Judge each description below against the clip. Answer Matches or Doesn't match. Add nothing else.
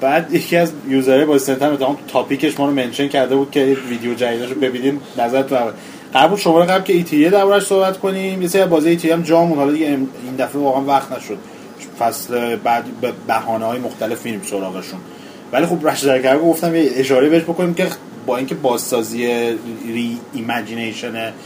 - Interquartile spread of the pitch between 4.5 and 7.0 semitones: Matches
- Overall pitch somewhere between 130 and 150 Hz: Matches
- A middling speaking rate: Doesn't match